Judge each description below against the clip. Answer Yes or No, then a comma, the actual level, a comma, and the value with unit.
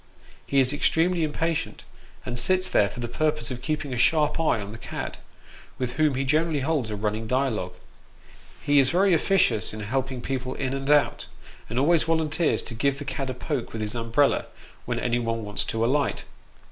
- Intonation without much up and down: No, average, 4.6 semitones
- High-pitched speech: No, low, 135 Hz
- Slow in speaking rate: No, average, 190 wpm